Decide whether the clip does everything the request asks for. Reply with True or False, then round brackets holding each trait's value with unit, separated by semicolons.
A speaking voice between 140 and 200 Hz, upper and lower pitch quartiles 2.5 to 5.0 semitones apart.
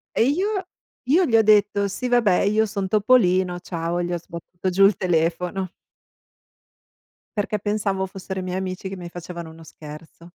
True (190 Hz; 2.9 semitones)